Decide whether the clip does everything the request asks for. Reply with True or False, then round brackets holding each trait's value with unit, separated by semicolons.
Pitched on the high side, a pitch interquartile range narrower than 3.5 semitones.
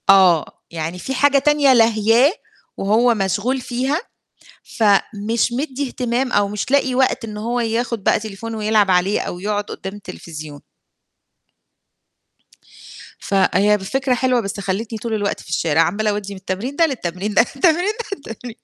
False (220 Hz; 4.3 semitones)